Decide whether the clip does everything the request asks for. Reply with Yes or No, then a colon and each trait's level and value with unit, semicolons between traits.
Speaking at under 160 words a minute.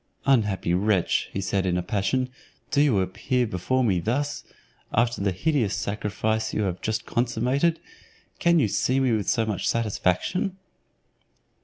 Yes: average, 150 wpm